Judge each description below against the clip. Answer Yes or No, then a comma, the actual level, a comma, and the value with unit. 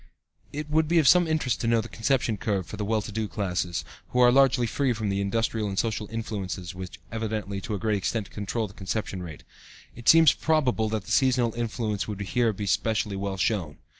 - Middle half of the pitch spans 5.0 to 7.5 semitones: No, average, 3.4 semitones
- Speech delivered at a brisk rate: Yes, fast, 215 wpm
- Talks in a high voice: No, low, 110 Hz